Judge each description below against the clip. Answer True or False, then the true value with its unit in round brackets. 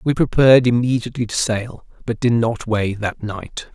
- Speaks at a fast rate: False (175 wpm)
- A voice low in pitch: True (115 Hz)